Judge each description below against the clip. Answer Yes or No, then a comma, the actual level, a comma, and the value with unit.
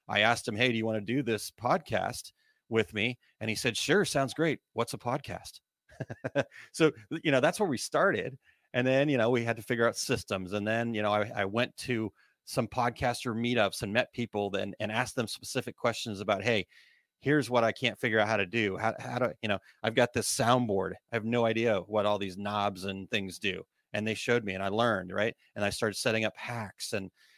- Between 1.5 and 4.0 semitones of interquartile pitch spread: Yes, average, 2.9 semitones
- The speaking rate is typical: No, fast, 230 wpm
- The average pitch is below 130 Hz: Yes, low, 115 Hz